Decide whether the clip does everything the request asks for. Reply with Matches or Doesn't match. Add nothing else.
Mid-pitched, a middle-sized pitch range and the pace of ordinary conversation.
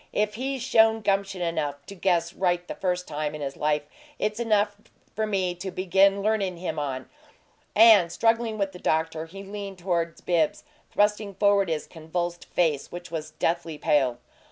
Matches